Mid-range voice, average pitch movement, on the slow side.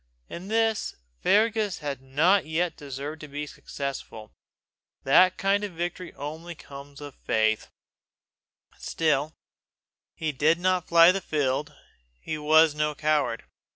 Yes: medium, 155 Hz; average, 3.8 semitones; slow, 125 wpm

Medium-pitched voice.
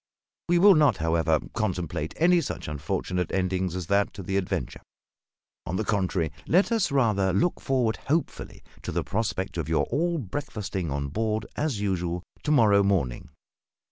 No: low, 100 Hz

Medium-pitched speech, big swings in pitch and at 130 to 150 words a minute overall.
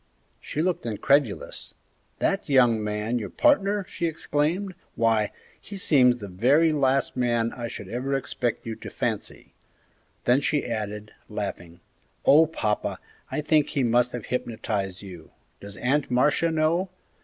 No: low, 125 Hz; wide, 5.7 semitones; average, 145 wpm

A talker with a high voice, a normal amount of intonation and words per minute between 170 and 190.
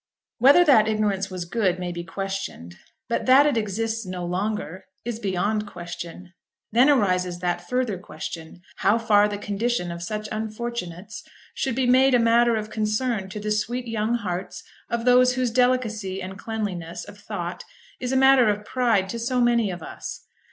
Yes: high, 215 Hz; average, 4.3 semitones; average, 175 wpm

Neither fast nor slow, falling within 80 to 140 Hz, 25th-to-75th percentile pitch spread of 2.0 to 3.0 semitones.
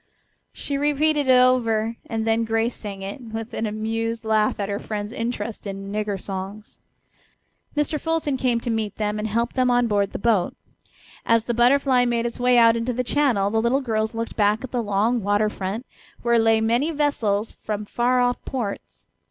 No: average, 190 wpm; high, 230 Hz; average, 2.7 semitones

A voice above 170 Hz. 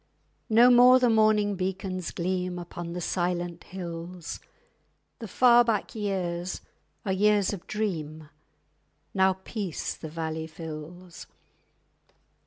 Yes: medium, 185 Hz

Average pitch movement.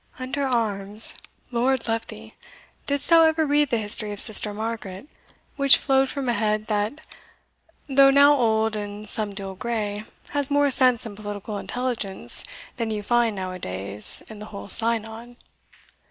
Yes: average, 4.2 semitones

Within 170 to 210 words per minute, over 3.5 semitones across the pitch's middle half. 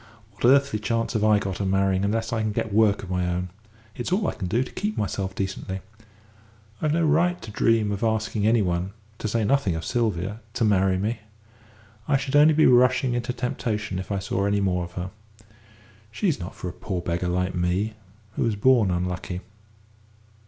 Yes: average, 200 wpm; average, 4.1 semitones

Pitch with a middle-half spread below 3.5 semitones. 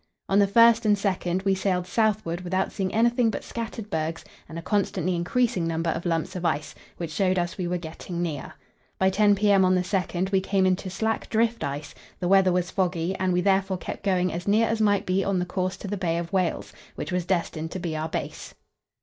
Yes: narrow, 2.5 semitones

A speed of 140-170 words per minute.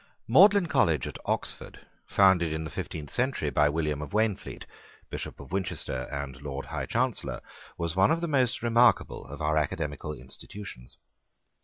Yes: average, 155 wpm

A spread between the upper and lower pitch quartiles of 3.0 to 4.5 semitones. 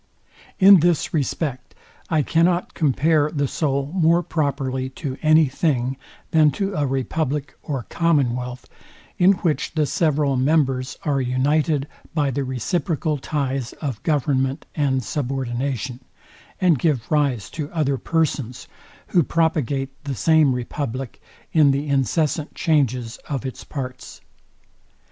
Yes: average, 3.3 semitones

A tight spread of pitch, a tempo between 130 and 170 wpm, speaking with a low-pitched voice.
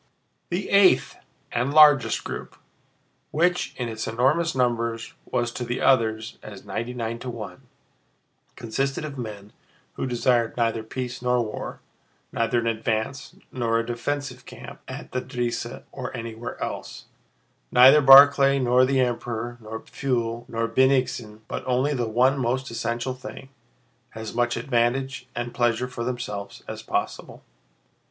Yes: narrow, 2.3 semitones; average, 140 wpm; low, 120 Hz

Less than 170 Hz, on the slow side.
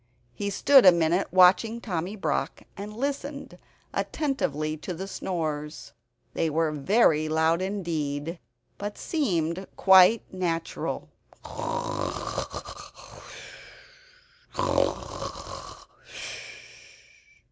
No: medium, 180 Hz; slow, 75 wpm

